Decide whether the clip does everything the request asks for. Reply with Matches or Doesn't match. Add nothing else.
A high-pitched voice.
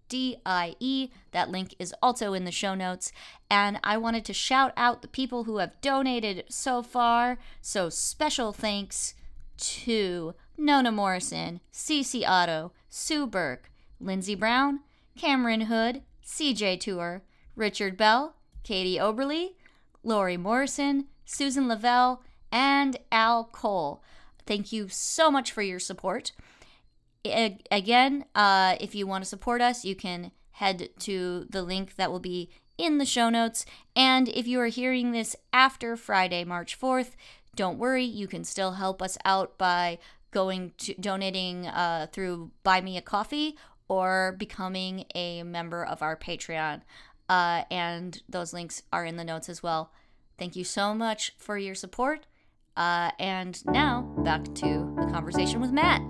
Matches